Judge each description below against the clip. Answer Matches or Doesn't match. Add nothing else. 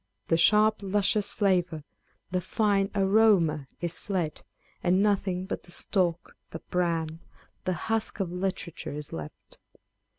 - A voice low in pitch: Doesn't match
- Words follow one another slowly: Matches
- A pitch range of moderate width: Matches